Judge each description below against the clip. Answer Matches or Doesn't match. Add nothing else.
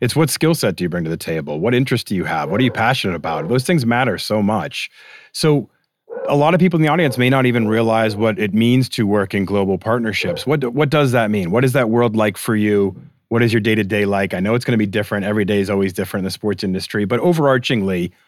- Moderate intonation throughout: Matches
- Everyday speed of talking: Doesn't match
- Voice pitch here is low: Matches